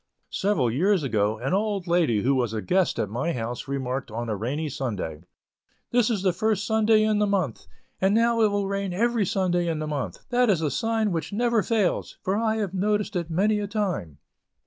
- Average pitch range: No, wide, 7.6 semitones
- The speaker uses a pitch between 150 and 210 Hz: Yes, medium, 185 Hz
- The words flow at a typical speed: No, fast, 210 wpm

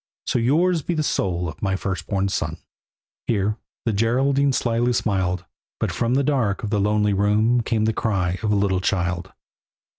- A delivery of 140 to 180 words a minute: Yes, average, 175 wpm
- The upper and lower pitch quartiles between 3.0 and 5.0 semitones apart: Yes, average, 3.9 semitones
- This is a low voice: Yes, low, 105 Hz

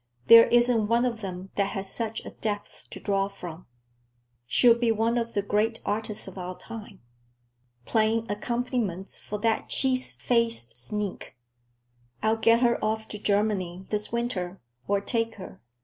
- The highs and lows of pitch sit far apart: No, average, 2.7 semitones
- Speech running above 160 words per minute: No, average, 155 wpm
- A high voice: Yes, high, 215 Hz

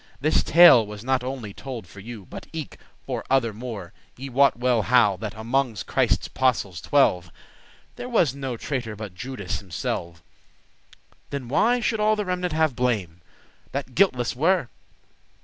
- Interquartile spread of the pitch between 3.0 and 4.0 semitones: No, average, 4.9 semitones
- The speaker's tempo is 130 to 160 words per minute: Yes, average, 155 wpm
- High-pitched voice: No, low, 125 Hz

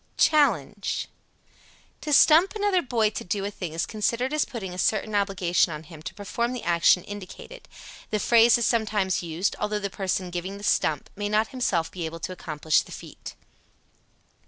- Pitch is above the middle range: Yes, high, 205 Hz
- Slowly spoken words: No, average, 180 wpm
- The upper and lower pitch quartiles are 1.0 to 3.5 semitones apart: No, average, 4.7 semitones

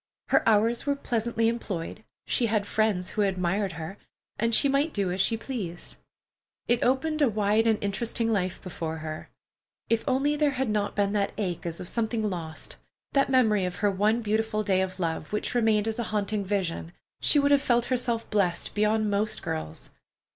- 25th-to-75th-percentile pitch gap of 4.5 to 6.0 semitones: No, average, 3.6 semitones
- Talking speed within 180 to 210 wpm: Yes, average, 185 wpm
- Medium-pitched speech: No, high, 215 Hz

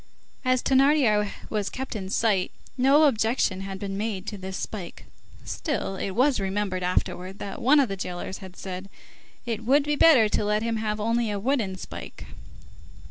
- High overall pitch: Yes, high, 210 Hz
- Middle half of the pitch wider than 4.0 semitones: Yes, average, 4.7 semitones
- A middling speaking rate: Yes, average, 175 wpm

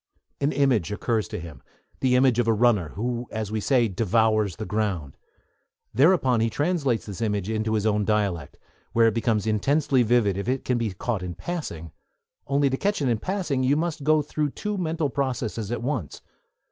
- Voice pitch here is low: Yes, low, 115 Hz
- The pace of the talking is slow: No, average, 190 wpm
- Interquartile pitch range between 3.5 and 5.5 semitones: Yes, average, 4.6 semitones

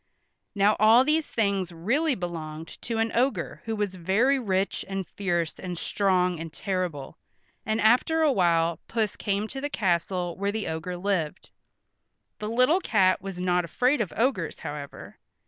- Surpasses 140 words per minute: Yes, average, 155 wpm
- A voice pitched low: No, high, 195 Hz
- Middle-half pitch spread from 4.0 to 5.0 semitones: Yes, average, 4.4 semitones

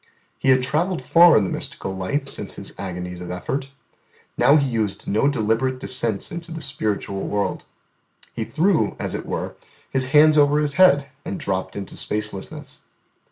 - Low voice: Yes, low, 130 Hz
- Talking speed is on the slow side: No, average, 165 wpm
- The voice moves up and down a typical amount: No, wide, 6.9 semitones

